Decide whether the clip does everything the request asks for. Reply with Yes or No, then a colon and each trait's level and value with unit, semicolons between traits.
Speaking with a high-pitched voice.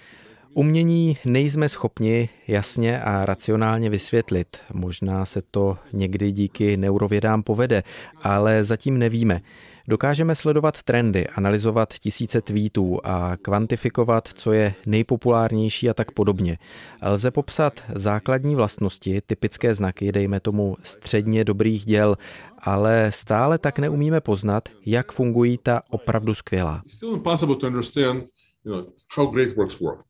No: low, 110 Hz